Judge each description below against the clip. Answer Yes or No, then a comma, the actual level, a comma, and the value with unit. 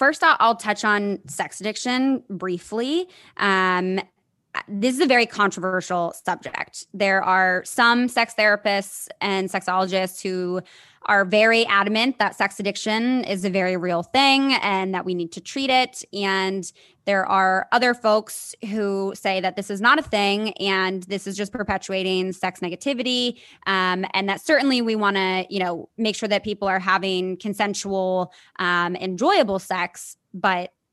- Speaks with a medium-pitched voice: No, high, 200 Hz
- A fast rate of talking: No, average, 155 wpm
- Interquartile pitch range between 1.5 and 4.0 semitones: Yes, average, 2.8 semitones